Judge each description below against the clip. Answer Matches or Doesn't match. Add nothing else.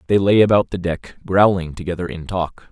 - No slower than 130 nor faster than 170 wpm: Doesn't match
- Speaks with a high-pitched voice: Doesn't match